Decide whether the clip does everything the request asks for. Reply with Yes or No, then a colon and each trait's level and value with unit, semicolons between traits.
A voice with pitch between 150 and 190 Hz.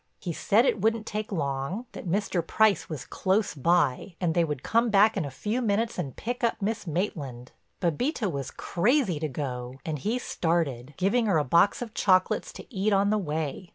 Yes: medium, 185 Hz